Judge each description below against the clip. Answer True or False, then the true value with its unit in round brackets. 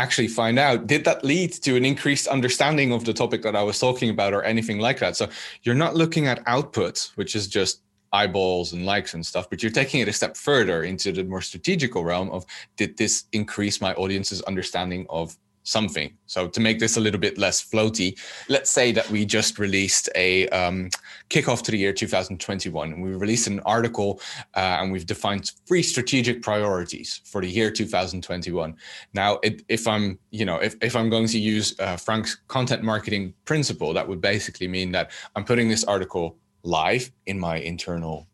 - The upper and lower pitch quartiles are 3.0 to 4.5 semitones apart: True (3.6 semitones)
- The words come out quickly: False (195 wpm)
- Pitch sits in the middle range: False (105 Hz)